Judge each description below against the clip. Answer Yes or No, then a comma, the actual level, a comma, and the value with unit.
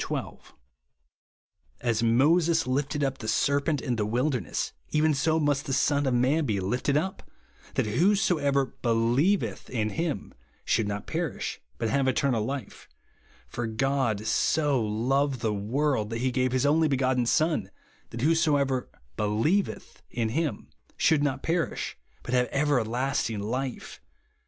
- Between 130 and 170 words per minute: Yes, average, 140 wpm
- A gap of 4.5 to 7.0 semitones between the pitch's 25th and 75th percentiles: No, average, 4.1 semitones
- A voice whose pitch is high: No, low, 135 Hz